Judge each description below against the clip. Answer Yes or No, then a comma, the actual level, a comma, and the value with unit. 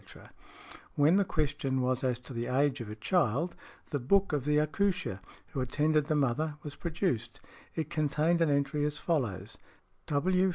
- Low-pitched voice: No, medium, 145 Hz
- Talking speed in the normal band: Yes, average, 170 wpm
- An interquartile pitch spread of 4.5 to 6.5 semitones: No, average, 3.7 semitones